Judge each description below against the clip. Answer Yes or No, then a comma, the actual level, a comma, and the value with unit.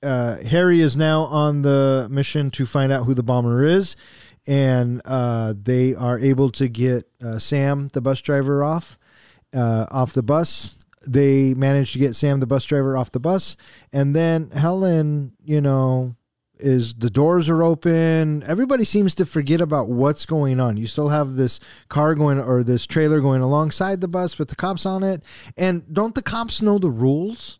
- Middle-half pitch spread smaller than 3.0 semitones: No, average, 3.8 semitones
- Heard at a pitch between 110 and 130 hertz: No, medium, 140 Hz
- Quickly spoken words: No, average, 185 wpm